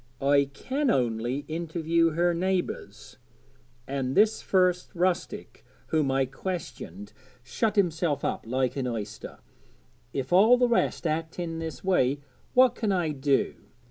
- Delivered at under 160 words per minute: Yes, slow, 135 wpm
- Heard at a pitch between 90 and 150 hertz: No, medium, 165 Hz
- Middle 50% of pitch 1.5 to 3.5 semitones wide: No, wide, 5.4 semitones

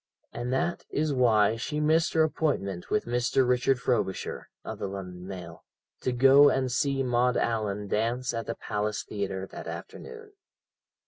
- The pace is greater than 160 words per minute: No, average, 155 wpm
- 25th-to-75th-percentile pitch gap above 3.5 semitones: Yes, average, 4.5 semitones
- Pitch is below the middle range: Yes, low, 120 Hz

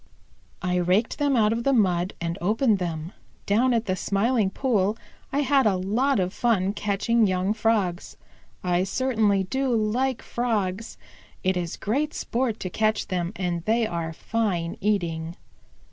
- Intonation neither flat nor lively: Yes, average, 4.2 semitones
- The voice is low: No, high, 210 Hz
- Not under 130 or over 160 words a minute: Yes, average, 155 wpm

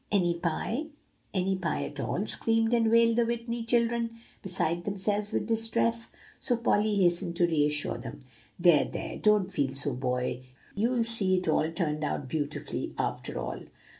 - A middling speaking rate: Yes, average, 160 wpm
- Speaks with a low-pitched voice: No, high, 195 Hz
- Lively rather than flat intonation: Yes, wide, 6.2 semitones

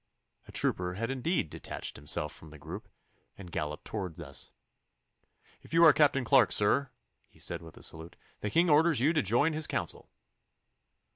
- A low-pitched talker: Yes, low, 115 Hz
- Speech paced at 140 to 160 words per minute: No, average, 170 wpm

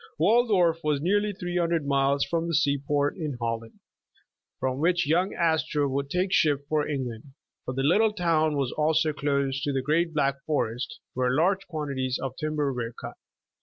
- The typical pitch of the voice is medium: Yes, medium, 150 Hz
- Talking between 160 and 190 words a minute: Yes, average, 175 wpm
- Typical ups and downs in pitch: Yes, average, 3.7 semitones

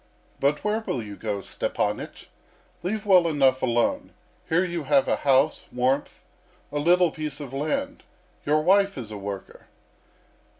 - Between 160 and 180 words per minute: No, average, 145 wpm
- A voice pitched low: No, medium, 145 Hz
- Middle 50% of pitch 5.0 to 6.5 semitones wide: Yes, wide, 5.5 semitones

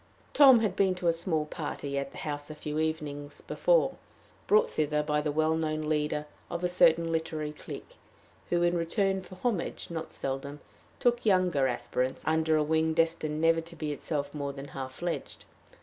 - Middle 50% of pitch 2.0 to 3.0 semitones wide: Yes, narrow, 2.5 semitones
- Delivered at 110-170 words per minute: No, average, 180 wpm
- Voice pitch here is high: No, medium, 160 Hz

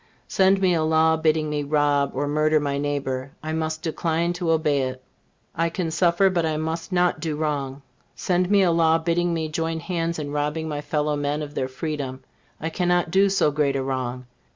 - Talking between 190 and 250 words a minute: Yes, average, 200 wpm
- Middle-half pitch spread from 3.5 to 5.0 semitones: No, narrow, 2.5 semitones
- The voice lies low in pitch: No, medium, 155 Hz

